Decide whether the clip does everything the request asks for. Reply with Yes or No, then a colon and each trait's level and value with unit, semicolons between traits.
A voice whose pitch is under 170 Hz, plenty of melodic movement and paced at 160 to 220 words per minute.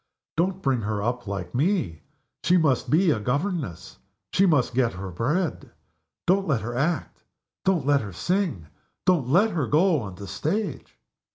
Yes: medium, 140 Hz; wide, 8.3 semitones; average, 165 wpm